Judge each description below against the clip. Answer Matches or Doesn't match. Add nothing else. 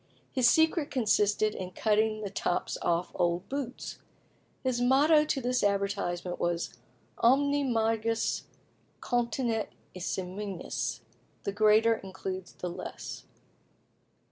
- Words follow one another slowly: Matches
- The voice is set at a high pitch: Matches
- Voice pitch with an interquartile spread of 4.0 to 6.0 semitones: Matches